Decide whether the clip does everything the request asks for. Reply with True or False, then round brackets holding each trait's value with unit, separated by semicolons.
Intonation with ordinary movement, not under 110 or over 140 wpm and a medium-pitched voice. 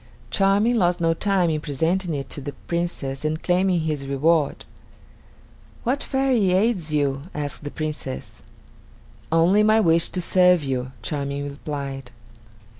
True (4.5 semitones; 135 wpm; 160 Hz)